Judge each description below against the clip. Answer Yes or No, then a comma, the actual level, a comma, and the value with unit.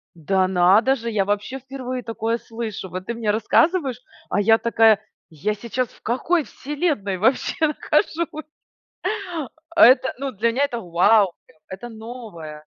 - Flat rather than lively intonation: No, average, 4.7 semitones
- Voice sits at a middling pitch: No, high, 230 Hz